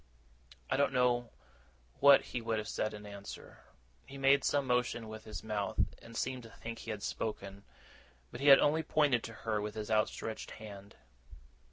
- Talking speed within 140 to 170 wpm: No, average, 180 wpm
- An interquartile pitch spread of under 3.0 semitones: No, average, 3.4 semitones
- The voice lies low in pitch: Yes, low, 115 Hz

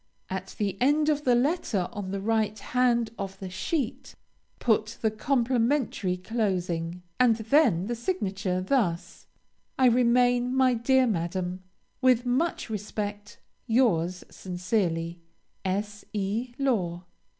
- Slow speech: Yes, slow, 120 wpm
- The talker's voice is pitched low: No, high, 220 Hz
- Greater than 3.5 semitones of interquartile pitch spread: Yes, average, 4.9 semitones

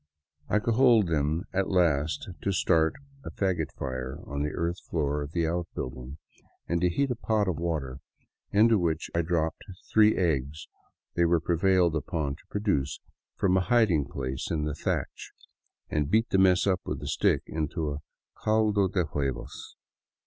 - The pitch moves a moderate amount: Yes, average, 4.5 semitones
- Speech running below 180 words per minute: Yes, average, 170 wpm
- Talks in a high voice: No, very low, 85 Hz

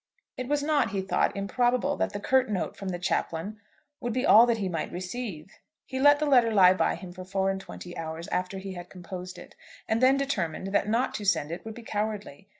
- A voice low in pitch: No, high, 200 Hz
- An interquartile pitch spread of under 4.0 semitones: No, average, 4.9 semitones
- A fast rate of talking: Yes, fast, 230 wpm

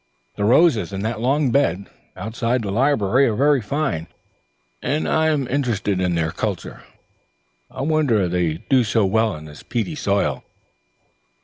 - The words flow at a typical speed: Yes, average, 150 wpm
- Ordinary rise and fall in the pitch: No, wide, 6.0 semitones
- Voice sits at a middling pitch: No, low, 115 Hz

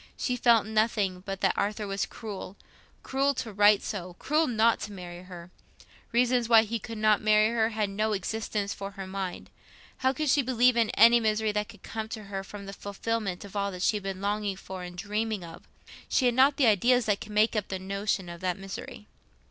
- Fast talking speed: Yes, fast, 210 wpm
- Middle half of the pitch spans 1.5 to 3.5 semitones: Yes, average, 2.7 semitones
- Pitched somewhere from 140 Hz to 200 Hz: No, high, 210 Hz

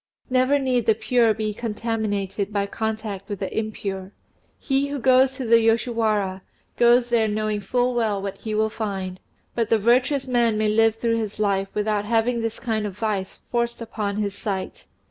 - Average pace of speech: Yes, average, 180 wpm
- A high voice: Yes, high, 220 Hz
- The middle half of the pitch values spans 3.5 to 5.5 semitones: No, narrow, 2.5 semitones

